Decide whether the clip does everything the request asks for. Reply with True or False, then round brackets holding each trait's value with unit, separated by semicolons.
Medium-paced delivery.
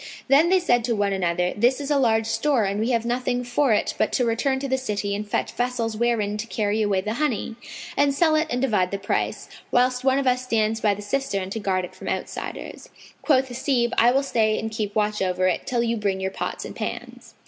False (240 wpm)